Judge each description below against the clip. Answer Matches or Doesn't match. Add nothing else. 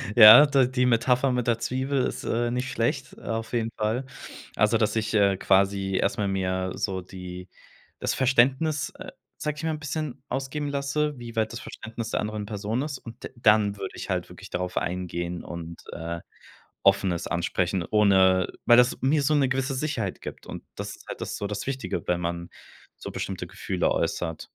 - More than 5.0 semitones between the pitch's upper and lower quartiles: Matches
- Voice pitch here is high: Doesn't match